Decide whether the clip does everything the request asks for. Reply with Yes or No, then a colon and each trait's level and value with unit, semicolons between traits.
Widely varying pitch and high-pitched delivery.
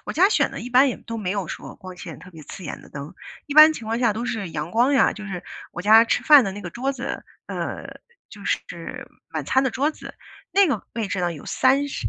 Yes: wide, 6.6 semitones; high, 225 Hz